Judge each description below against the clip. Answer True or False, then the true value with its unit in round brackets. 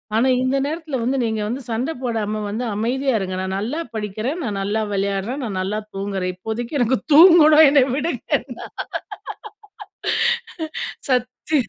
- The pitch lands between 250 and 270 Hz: False (235 Hz)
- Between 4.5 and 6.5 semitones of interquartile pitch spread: True (5.1 semitones)